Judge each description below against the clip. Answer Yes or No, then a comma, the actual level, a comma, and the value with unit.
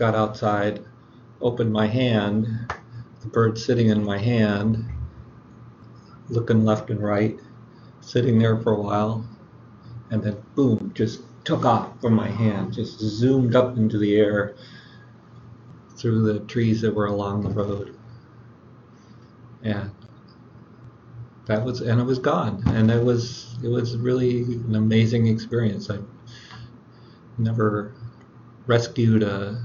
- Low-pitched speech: Yes, low, 115 Hz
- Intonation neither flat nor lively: No, narrow, 1.8 semitones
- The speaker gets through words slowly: Yes, slow, 130 wpm